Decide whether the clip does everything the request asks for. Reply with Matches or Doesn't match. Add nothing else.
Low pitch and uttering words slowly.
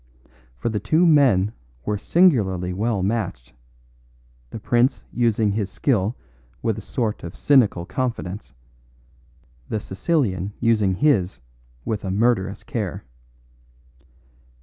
Matches